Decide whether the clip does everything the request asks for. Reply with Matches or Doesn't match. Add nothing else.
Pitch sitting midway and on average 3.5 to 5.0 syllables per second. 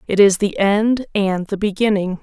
Doesn't match